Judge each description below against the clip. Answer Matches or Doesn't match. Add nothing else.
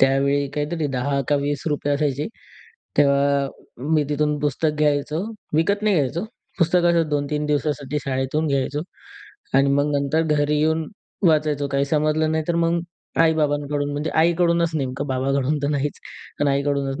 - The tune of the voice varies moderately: Doesn't match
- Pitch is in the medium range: Matches